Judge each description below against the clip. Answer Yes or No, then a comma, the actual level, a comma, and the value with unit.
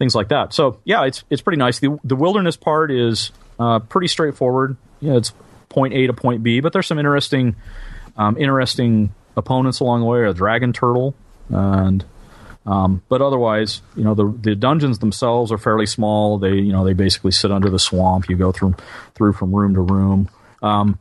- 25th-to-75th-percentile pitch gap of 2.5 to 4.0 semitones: No, average, 4.5 semitones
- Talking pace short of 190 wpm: No, average, 195 wpm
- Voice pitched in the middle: No, low, 110 Hz